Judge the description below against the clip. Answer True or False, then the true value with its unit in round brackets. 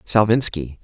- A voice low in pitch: True (100 Hz)